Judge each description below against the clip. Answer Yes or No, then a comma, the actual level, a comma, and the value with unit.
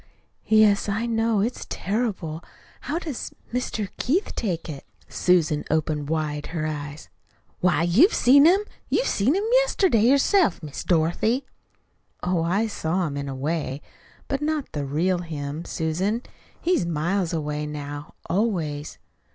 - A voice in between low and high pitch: Yes, medium, 180 Hz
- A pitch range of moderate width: No, wide, 7.1 semitones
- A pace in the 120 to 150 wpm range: Yes, average, 140 wpm